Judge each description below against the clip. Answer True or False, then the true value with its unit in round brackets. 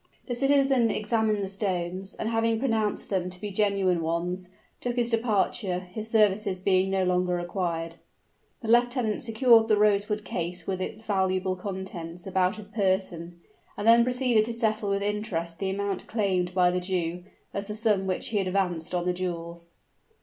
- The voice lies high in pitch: True (195 Hz)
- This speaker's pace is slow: False (175 wpm)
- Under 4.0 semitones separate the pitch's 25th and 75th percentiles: True (3.2 semitones)